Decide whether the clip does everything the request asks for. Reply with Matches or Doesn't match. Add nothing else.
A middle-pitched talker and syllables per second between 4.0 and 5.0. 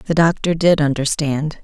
Matches